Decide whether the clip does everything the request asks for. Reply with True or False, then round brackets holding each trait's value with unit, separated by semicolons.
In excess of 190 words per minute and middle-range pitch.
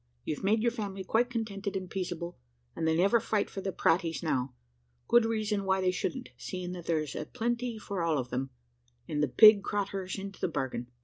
False (200 wpm; 195 Hz)